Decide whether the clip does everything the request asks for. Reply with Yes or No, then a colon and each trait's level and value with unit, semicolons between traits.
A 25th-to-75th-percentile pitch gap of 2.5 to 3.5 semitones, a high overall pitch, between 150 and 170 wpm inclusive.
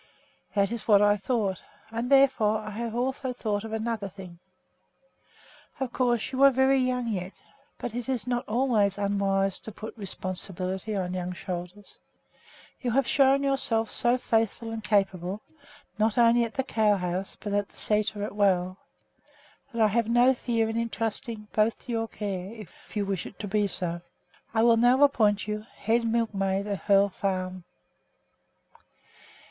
Yes: average, 3.1 semitones; high, 215 Hz; average, 165 wpm